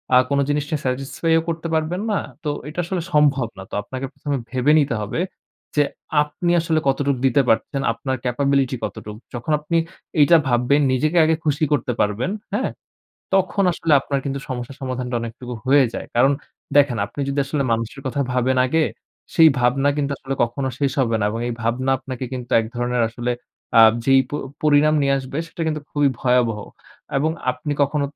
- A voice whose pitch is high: No, low, 135 Hz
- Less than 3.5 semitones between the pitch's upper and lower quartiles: Yes, average, 3.1 semitones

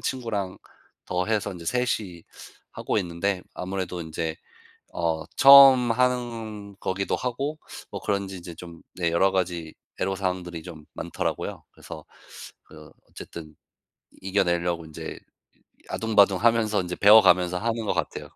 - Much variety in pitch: No, average, 4.3 semitones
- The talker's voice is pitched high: No, very low, 95 Hz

